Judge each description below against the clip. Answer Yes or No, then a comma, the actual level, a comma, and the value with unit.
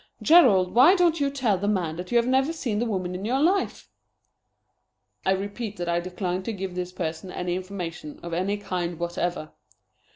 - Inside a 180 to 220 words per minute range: Yes, average, 190 wpm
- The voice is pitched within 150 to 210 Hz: Yes, high, 190 Hz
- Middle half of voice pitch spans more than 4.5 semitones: Yes, average, 5.1 semitones